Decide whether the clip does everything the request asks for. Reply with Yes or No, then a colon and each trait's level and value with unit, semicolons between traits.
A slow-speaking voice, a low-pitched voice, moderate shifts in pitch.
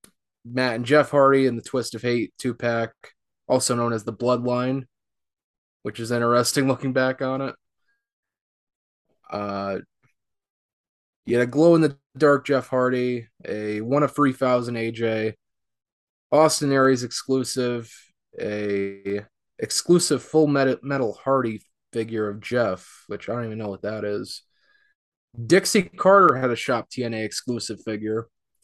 Yes: slow, 120 wpm; low, 125 Hz; average, 3.5 semitones